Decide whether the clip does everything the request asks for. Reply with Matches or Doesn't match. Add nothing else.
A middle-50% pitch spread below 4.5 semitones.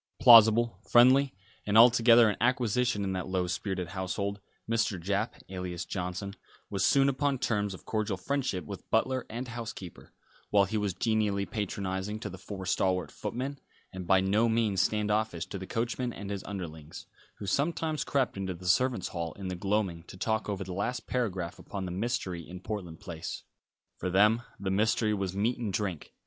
Matches